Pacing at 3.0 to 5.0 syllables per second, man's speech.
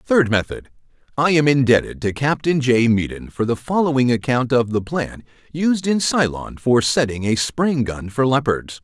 Yes: 4.6 syllables/s; male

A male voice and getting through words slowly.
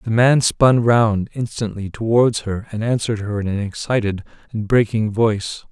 No: male; average, 170 wpm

